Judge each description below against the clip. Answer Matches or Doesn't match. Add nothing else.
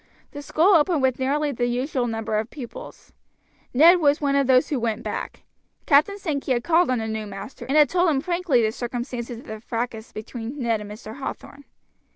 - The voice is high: Matches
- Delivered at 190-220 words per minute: Matches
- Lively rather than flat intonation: Doesn't match